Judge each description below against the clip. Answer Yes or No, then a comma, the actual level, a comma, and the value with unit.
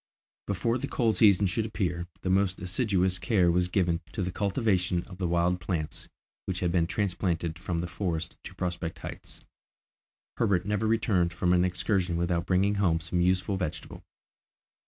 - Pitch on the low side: Yes, very low, 90 Hz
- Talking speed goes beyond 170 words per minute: No, average, 165 wpm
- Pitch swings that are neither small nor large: No, narrow, 2.3 semitones